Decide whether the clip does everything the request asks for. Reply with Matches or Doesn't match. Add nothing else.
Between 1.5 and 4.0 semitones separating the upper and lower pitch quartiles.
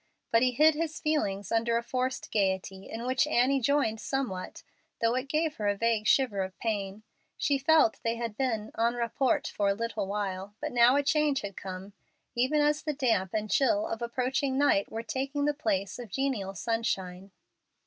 Doesn't match